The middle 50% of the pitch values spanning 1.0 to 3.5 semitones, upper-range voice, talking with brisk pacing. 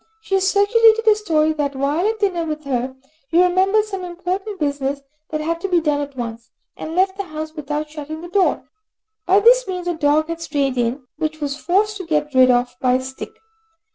No: average, 5.0 semitones; very high, 315 Hz; fast, 215 wpm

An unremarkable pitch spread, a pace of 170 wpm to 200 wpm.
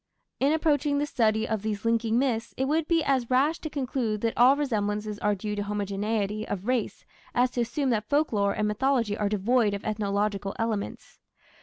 Yes: average, 4.1 semitones; average, 185 wpm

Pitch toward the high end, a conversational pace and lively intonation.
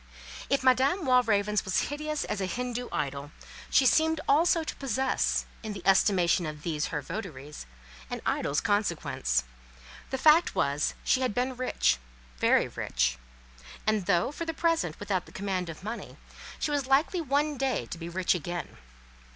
Yes: high, 210 Hz; average, 160 wpm; wide, 8.5 semitones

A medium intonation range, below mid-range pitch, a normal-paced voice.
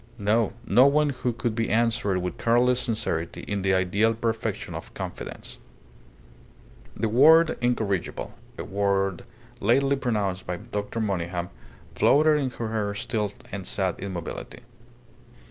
No: average, 3.8 semitones; low, 110 Hz; slow, 130 wpm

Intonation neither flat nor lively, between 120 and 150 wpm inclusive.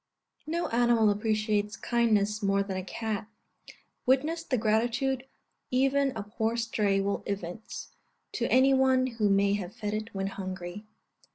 Yes: average, 3.6 semitones; average, 145 wpm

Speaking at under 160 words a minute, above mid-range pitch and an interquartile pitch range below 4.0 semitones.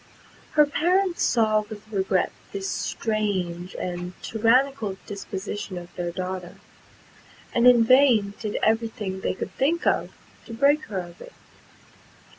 No: slow, 135 wpm; high, 215 Hz; average, 4.8 semitones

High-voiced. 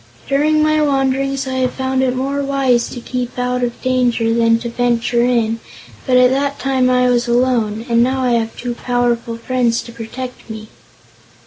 Yes: very high, 250 Hz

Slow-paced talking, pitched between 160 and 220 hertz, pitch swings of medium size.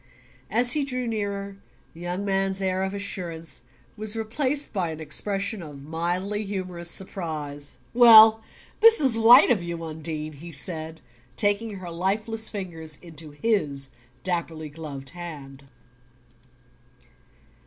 Yes: slow, 125 wpm; medium, 185 Hz; average, 4.9 semitones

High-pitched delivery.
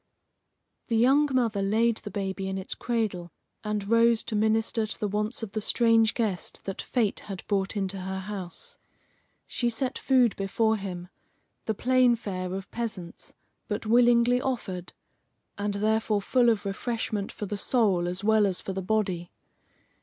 Yes: high, 215 Hz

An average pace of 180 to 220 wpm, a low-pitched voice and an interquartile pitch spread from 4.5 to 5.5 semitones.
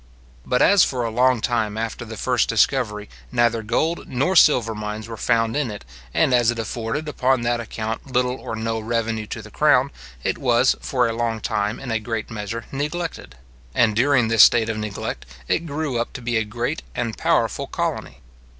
No: average, 195 wpm; low, 115 Hz; narrow, 2.4 semitones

